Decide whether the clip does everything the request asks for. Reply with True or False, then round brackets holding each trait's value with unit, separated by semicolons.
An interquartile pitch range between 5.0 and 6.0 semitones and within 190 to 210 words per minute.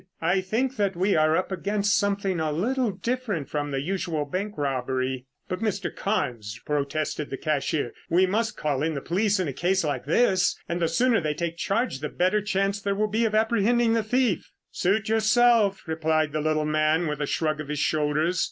True (5.6 semitones; 200 wpm)